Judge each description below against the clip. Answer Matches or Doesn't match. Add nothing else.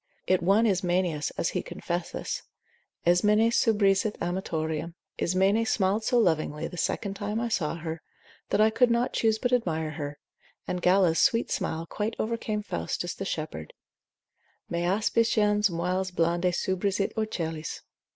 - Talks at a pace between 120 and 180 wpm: Matches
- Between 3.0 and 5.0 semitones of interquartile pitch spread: Matches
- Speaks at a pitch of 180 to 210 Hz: Matches